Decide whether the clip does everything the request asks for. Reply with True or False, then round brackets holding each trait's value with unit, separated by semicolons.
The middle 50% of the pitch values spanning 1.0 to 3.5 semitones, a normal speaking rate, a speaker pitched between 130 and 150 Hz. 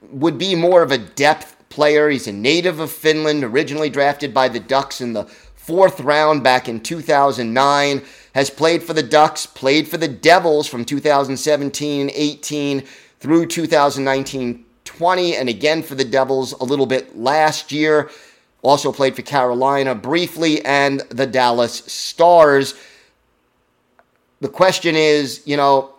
True (2.5 semitones; 145 wpm; 140 Hz)